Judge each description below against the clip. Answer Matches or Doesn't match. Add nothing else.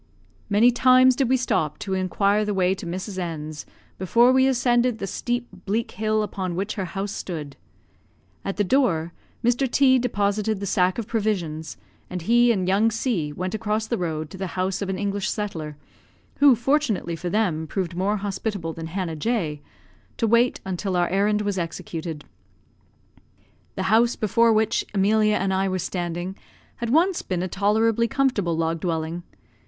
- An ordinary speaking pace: Matches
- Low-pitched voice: Doesn't match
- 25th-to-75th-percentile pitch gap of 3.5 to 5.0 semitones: Matches